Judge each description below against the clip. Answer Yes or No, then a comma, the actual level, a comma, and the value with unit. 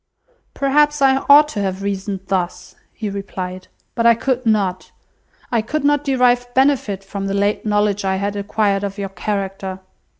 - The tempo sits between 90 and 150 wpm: No, average, 165 wpm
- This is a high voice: Yes, high, 205 Hz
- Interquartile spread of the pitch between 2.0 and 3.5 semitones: No, average, 4.0 semitones